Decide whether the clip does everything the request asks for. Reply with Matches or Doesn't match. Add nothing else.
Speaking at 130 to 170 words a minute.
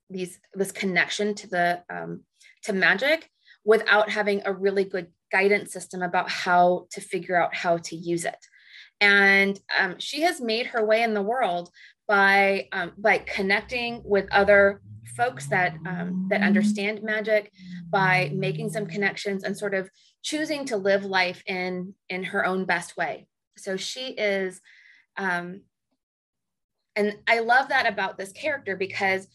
Matches